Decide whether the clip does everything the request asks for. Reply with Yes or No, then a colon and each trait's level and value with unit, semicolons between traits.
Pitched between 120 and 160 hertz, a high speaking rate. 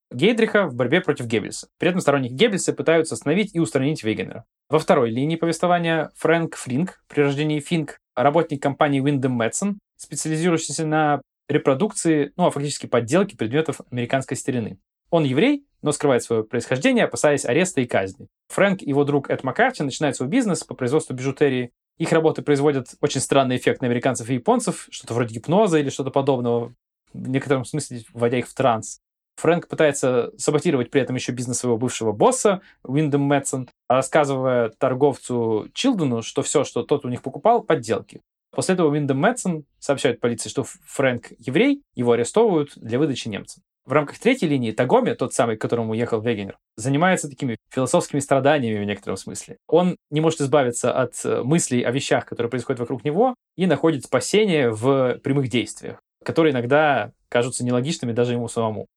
Yes: medium, 140 Hz; fast, 165 wpm